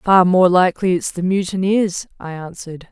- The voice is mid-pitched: Yes, medium, 180 Hz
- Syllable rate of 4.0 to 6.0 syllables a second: Yes, 5.1 syllables/s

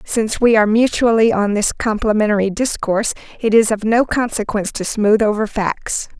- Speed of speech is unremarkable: Yes, average, 165 wpm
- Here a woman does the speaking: Yes, female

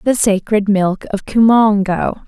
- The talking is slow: Yes, slow, 130 wpm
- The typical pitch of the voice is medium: No, high, 205 Hz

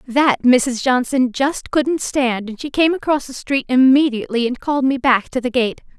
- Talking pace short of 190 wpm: No, average, 200 wpm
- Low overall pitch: No, very high, 260 Hz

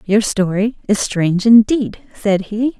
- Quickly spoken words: No, average, 150 wpm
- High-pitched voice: Yes, high, 210 Hz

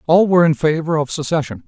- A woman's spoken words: No, male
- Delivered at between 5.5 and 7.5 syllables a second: Yes, 6.5 syllables/s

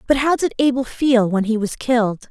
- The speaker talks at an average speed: No, fast, 235 wpm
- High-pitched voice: Yes, high, 240 Hz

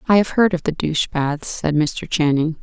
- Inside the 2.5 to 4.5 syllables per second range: No, 4.9 syllables/s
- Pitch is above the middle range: No, medium, 160 Hz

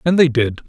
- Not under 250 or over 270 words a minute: Yes, fast, 265 wpm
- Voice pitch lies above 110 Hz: Yes, medium, 140 Hz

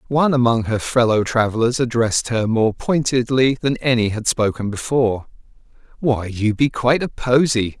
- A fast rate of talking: No, average, 155 wpm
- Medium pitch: No, low, 120 Hz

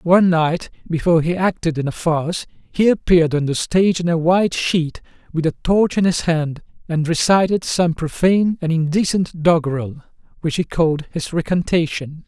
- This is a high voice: No, medium, 165 Hz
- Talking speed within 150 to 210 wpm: Yes, average, 170 wpm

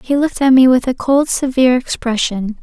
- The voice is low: No, very high, 255 Hz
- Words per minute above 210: No, fast, 205 wpm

